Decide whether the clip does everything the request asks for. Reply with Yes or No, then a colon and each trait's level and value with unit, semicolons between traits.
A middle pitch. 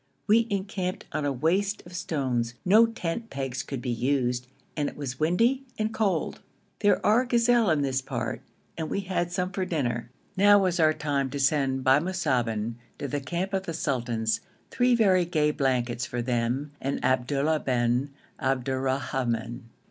Yes: medium, 145 Hz